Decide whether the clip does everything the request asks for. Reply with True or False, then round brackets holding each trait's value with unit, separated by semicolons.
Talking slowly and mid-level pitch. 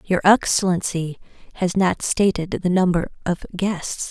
True (130 wpm; 180 Hz)